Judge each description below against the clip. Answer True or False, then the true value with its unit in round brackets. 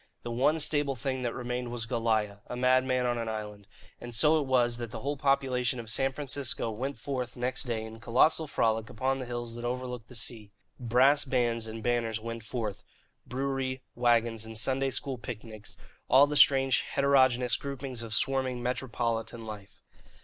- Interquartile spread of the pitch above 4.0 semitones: False (2.5 semitones)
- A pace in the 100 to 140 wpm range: False (175 wpm)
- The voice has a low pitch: True (125 Hz)